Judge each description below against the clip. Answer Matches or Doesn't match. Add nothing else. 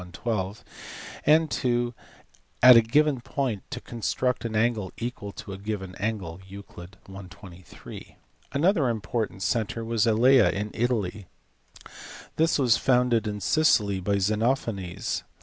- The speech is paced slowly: Matches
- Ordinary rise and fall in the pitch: Matches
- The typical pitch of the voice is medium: Doesn't match